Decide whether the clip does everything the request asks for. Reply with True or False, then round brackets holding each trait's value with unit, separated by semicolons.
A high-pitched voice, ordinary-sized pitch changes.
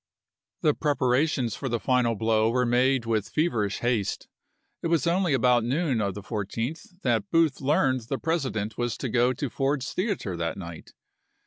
False (125 Hz; 4.3 semitones)